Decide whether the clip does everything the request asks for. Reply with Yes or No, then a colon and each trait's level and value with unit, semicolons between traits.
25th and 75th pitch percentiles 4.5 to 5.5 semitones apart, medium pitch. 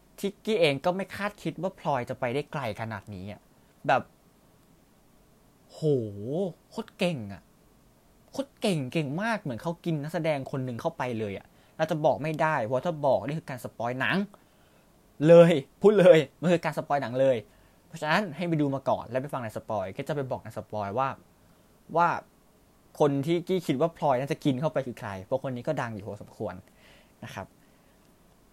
Yes: average, 5.2 semitones; medium, 145 Hz